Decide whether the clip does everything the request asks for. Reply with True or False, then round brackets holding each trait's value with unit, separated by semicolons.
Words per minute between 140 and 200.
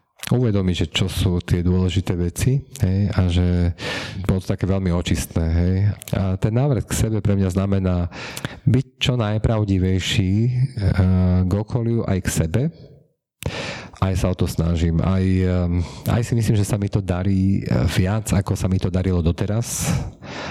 True (155 wpm)